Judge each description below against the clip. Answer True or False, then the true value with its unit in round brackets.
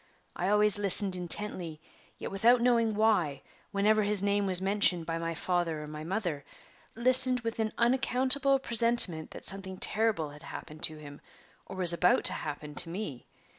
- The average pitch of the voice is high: True (195 Hz)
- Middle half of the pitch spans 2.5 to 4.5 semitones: False (5.1 semitones)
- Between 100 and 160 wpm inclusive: False (170 wpm)